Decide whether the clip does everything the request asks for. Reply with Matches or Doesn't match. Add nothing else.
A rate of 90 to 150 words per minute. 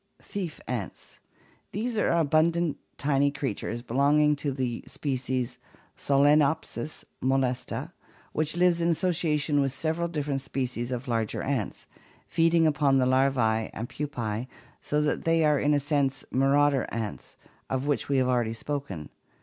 Matches